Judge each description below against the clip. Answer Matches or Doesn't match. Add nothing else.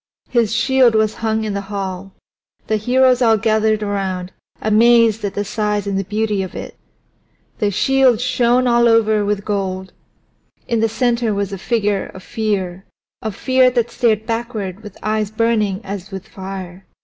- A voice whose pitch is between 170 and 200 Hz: Doesn't match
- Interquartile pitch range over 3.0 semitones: Doesn't match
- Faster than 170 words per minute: Doesn't match